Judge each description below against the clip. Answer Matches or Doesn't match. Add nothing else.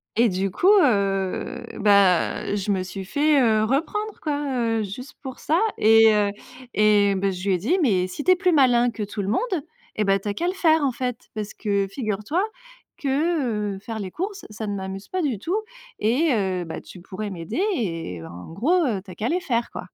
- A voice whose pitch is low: Doesn't match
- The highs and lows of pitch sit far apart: Matches